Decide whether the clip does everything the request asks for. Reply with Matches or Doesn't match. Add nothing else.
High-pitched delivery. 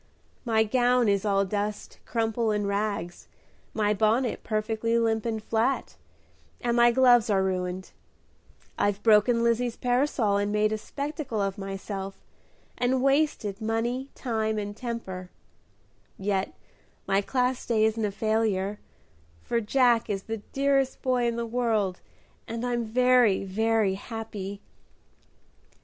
Matches